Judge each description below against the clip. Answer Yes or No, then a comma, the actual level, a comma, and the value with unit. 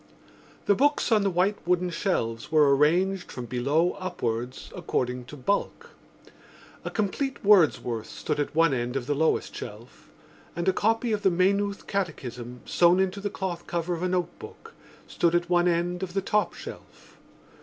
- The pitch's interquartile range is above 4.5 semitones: Yes, average, 5.0 semitones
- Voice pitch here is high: No, medium, 175 Hz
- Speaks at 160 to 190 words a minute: Yes, average, 165 wpm